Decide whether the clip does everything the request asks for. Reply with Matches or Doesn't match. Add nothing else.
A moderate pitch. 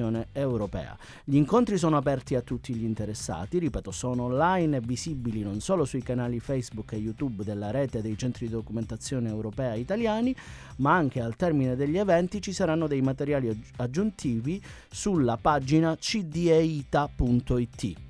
Doesn't match